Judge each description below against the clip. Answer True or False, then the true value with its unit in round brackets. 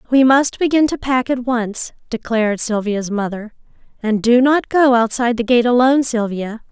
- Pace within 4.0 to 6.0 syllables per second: True (5.0 syllables/s)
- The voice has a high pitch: True (240 Hz)